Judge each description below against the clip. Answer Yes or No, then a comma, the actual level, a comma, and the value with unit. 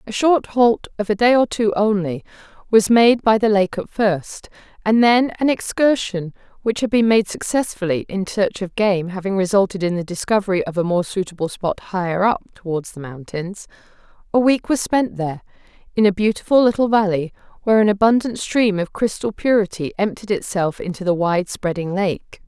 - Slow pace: No, average, 180 wpm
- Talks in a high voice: Yes, high, 200 Hz